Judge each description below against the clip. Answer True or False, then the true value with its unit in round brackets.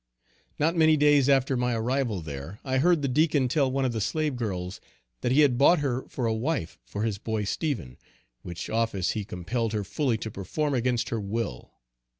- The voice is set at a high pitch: False (120 Hz)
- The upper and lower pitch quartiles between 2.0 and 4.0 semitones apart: False (5.0 semitones)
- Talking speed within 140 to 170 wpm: False (195 wpm)